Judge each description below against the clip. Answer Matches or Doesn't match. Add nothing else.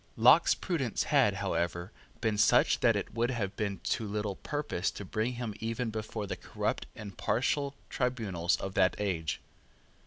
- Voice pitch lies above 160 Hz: Doesn't match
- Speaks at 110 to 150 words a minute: Doesn't match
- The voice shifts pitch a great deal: Doesn't match